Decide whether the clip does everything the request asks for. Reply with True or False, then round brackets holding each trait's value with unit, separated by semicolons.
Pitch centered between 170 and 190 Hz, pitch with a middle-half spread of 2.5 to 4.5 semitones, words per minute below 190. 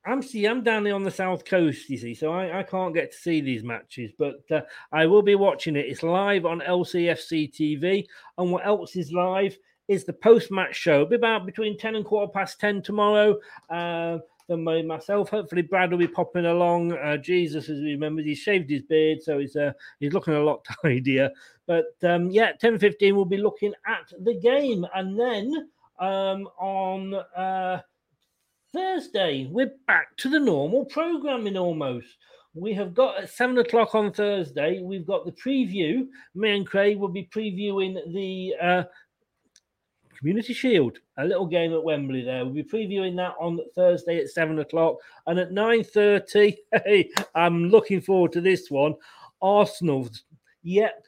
True (185 Hz; 4.2 semitones; 175 wpm)